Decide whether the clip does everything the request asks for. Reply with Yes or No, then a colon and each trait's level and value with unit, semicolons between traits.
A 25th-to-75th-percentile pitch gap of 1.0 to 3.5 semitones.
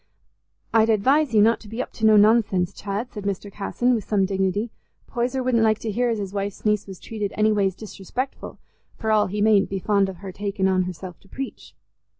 Yes: narrow, 2.4 semitones